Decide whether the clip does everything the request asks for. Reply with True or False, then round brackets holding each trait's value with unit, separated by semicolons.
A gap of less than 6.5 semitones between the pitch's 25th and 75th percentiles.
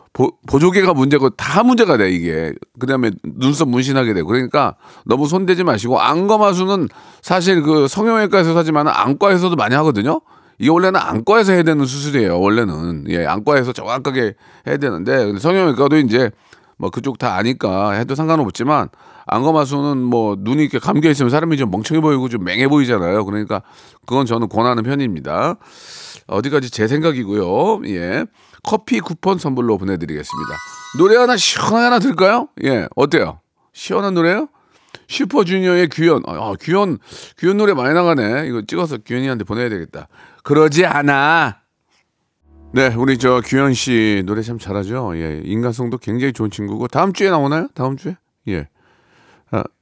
False (7.1 semitones)